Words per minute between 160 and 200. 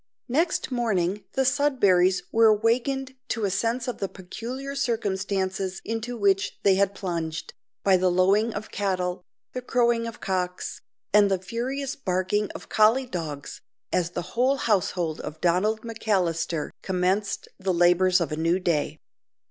No: average, 145 wpm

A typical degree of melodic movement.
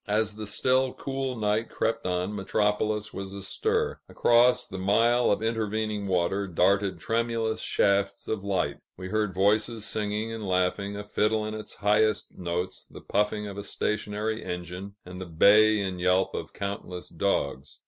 No: narrow, 2.3 semitones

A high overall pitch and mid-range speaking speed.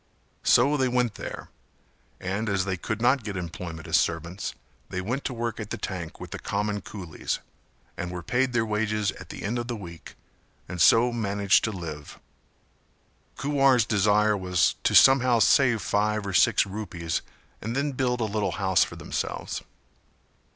No: low, 105 Hz; average, 170 wpm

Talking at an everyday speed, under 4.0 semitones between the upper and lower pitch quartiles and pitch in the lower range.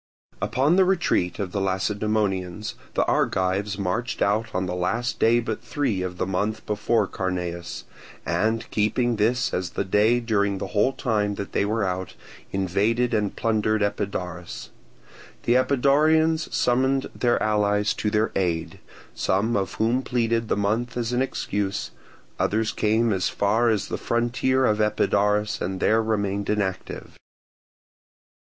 Yes: average, 145 wpm; average, 3.1 semitones; low, 105 Hz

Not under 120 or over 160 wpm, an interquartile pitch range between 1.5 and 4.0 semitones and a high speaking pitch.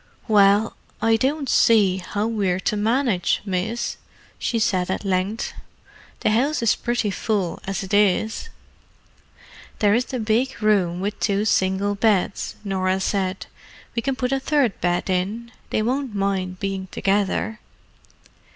Yes: average, 140 wpm; average, 3.3 semitones; high, 205 Hz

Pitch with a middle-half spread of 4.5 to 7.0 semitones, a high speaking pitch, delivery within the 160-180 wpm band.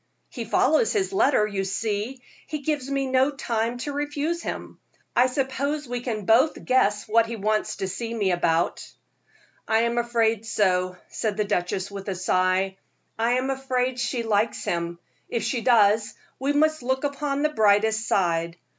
Yes: average, 4.8 semitones; high, 230 Hz; average, 170 wpm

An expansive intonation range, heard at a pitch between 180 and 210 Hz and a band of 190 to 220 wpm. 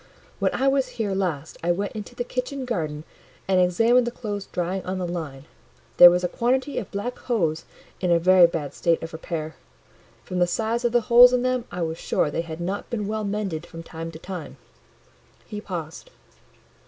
Yes: wide, 5.9 semitones; medium, 185 Hz; average, 200 wpm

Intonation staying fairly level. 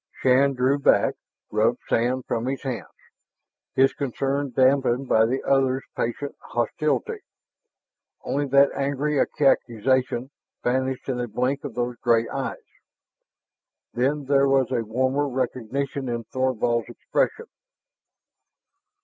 Yes: narrow, 2.1 semitones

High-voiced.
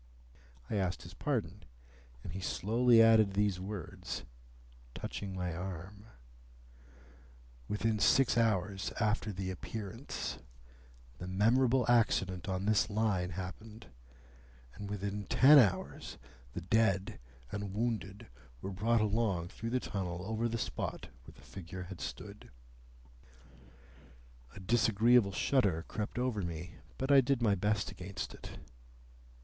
No: low, 105 Hz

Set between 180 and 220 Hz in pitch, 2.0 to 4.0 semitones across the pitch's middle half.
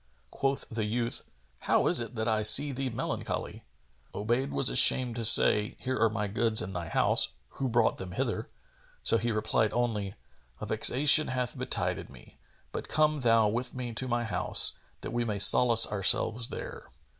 No: low, 115 Hz; narrow, 2.6 semitones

